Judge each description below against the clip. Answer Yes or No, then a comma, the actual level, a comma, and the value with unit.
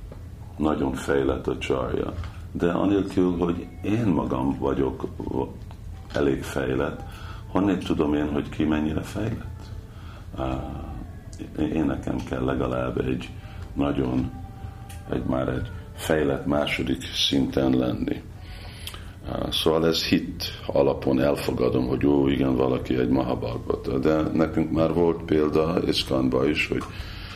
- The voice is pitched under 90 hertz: Yes, very low, 80 Hz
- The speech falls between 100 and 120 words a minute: Yes, average, 110 wpm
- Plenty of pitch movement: Yes, wide, 5.9 semitones